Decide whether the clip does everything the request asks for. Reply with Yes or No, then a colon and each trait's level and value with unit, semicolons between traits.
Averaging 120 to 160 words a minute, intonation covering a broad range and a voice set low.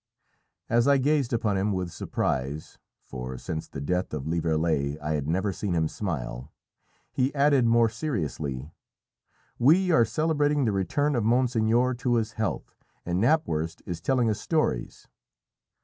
Yes: average, 150 wpm; wide, 8.3 semitones; low, 105 Hz